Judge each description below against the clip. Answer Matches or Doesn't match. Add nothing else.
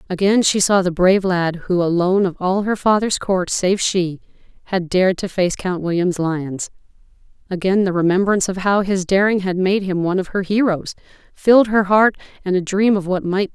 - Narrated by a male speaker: Doesn't match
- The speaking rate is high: Matches